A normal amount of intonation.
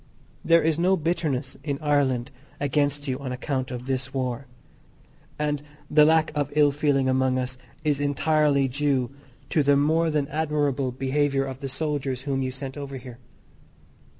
No: narrow, 2.2 semitones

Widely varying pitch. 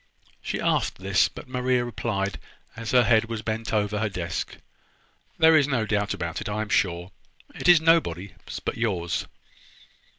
No: average, 3.9 semitones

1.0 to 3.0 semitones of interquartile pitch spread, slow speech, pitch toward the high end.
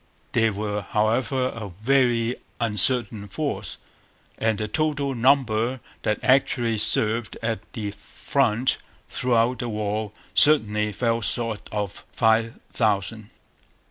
No: average, 2.7 semitones; slow, 110 wpm; low, 115 Hz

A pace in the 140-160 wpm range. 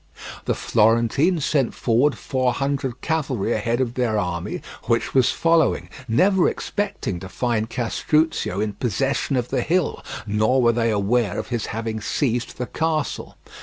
Yes: average, 150 wpm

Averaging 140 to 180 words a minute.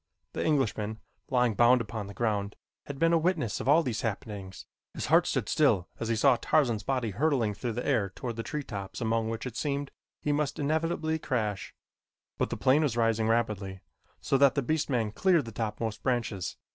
No: average, 200 wpm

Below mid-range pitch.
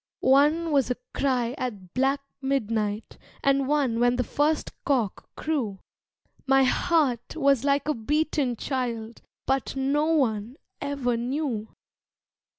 No: very high, 265 Hz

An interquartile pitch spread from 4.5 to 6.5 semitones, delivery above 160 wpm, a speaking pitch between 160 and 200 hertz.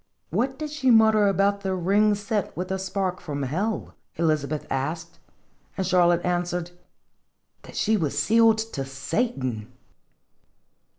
No: average, 4.8 semitones; average, 140 wpm; medium, 185 Hz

